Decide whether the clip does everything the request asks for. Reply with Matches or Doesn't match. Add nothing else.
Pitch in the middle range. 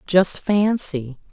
Matches